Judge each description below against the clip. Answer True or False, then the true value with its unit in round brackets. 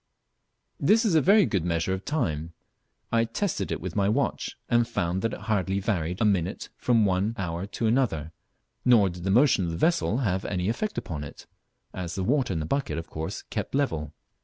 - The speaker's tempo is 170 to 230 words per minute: True (205 wpm)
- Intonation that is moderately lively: False (5.7 semitones)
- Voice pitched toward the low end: True (100 Hz)